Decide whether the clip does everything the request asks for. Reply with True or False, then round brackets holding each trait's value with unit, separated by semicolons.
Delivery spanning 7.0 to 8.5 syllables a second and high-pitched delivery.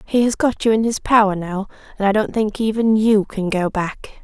False (5.0 syllables/s; 210 Hz)